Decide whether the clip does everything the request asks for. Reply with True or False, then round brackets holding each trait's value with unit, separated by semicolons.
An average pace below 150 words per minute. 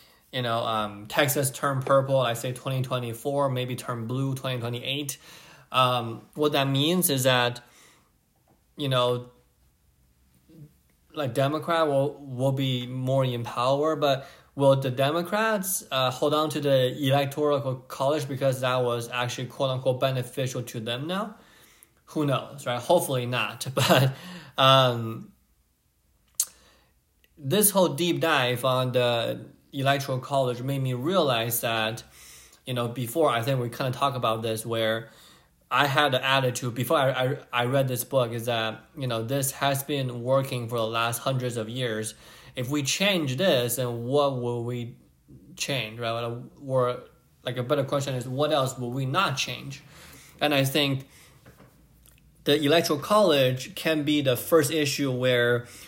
False (155 wpm)